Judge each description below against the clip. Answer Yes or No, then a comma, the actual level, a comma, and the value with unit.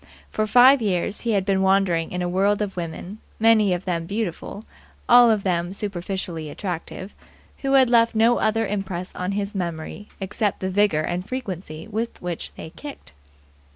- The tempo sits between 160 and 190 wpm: Yes, average, 175 wpm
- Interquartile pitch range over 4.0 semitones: No, average, 3.5 semitones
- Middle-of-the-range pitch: No, high, 195 Hz